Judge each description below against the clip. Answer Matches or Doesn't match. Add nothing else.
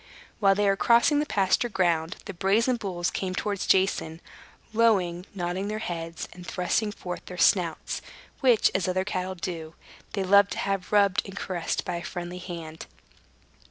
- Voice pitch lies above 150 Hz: Matches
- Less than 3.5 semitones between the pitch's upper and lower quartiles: Matches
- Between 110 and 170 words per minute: Matches